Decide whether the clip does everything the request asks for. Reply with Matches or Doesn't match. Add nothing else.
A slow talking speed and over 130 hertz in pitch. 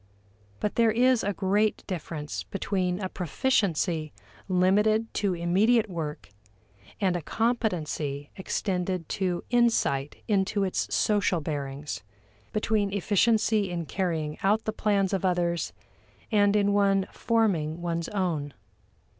Matches